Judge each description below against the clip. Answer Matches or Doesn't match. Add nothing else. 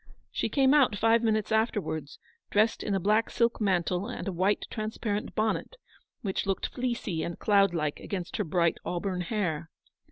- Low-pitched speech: Doesn't match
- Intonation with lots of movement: Doesn't match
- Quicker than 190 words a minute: Doesn't match